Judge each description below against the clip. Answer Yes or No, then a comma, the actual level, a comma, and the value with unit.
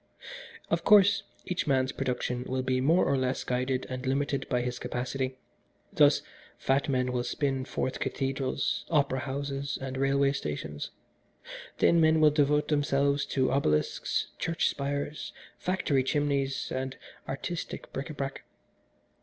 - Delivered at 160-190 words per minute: No, slow, 135 wpm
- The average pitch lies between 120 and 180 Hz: Yes, low, 135 Hz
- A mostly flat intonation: Yes, narrow, 1.7 semitones